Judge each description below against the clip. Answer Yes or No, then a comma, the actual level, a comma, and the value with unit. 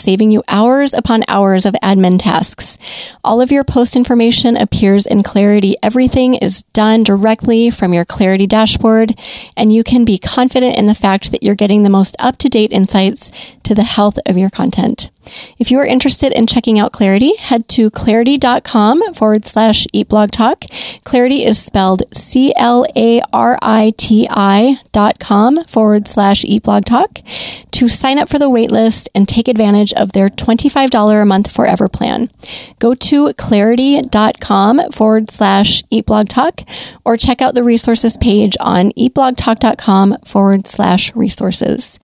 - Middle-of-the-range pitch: No, high, 220 Hz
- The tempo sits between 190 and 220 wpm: No, average, 155 wpm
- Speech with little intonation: No, average, 3.2 semitones